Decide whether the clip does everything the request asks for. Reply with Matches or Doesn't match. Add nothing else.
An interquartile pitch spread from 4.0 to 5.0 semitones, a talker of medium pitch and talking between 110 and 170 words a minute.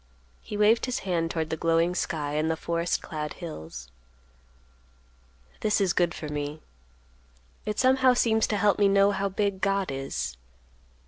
Matches